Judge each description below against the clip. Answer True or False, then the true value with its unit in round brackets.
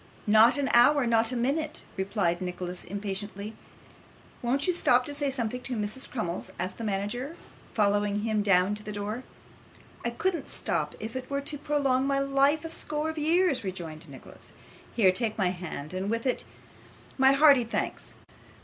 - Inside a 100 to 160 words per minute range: False (170 wpm)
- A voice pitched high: True (230 Hz)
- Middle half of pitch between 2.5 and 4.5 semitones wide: False (5.4 semitones)